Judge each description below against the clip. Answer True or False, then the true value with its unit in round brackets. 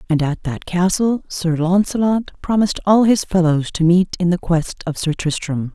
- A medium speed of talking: True (190 wpm)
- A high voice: False (180 Hz)